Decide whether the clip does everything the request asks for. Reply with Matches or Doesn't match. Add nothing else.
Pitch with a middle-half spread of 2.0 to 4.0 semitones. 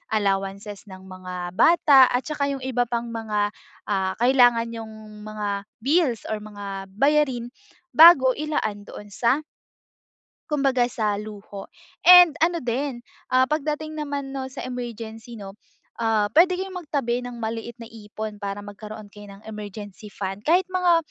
Doesn't match